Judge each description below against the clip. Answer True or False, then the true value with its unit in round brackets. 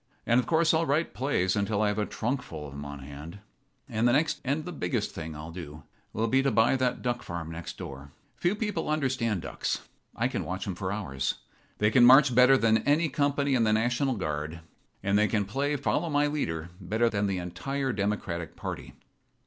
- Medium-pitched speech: False (110 Hz)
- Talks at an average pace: False (215 wpm)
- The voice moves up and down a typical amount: False (7.5 semitones)